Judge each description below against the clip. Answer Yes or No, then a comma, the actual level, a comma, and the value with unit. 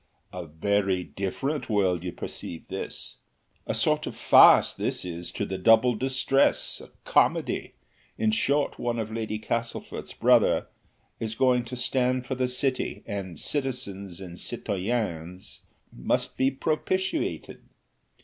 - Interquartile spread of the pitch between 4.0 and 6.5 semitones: Yes, average, 5.3 semitones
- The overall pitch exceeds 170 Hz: No, low, 110 Hz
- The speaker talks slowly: Yes, slow, 130 wpm